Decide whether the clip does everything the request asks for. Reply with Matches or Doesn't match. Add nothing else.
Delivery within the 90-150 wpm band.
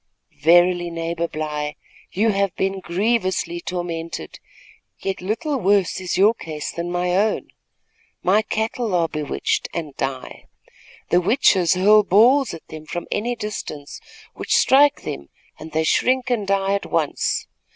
Matches